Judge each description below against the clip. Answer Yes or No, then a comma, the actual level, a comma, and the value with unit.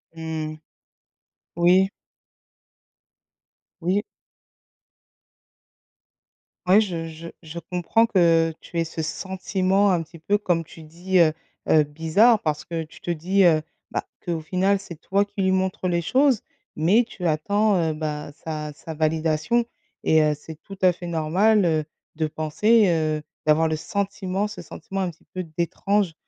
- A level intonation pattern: No, average, 3.5 semitones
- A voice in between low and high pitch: Yes, medium, 170 Hz